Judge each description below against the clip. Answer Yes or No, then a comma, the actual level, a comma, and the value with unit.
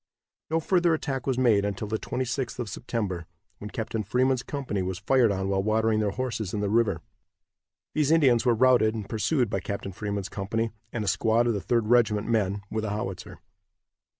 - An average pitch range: Yes, average, 3.5 semitones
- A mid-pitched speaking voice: No, low, 110 Hz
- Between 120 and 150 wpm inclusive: No, average, 190 wpm